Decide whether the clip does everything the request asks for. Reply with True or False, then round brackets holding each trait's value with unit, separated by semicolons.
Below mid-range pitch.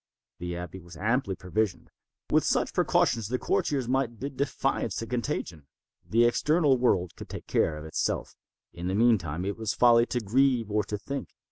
True (115 Hz)